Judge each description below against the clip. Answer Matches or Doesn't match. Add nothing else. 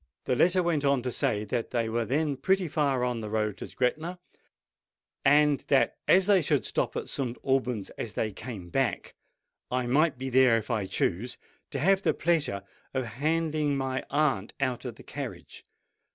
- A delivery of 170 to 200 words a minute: Matches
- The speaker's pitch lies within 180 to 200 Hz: Doesn't match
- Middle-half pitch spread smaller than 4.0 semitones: Doesn't match